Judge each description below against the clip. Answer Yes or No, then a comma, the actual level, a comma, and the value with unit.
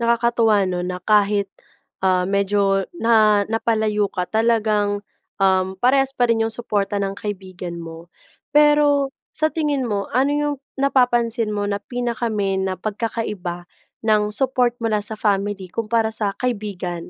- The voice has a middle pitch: No, high, 215 Hz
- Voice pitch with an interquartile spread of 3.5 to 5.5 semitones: No, average, 2.9 semitones